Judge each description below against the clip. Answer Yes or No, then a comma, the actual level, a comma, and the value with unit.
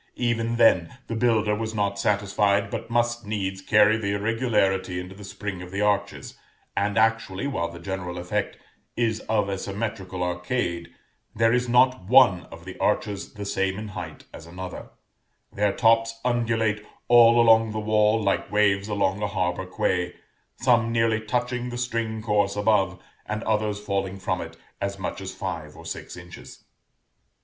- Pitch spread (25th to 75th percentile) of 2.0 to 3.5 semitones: Yes, average, 2.9 semitones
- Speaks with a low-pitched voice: Yes, low, 105 Hz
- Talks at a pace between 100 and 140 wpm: No, average, 165 wpm